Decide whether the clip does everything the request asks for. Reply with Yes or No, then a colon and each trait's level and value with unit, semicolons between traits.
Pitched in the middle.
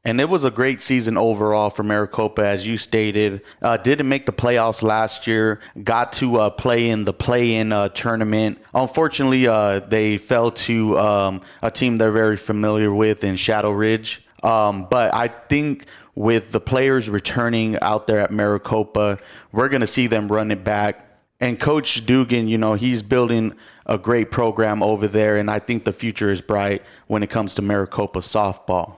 No: low, 110 Hz